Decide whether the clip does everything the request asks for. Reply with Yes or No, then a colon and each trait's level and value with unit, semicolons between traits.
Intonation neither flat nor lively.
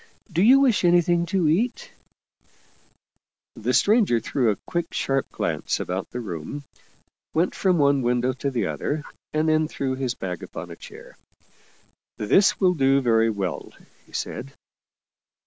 No: wide, 6.5 semitones